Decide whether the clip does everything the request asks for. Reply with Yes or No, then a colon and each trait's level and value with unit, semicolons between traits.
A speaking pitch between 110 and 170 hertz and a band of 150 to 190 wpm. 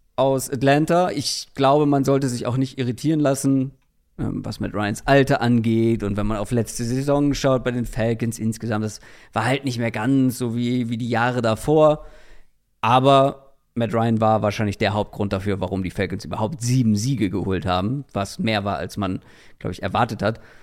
Yes: low, 120 Hz; average, 185 wpm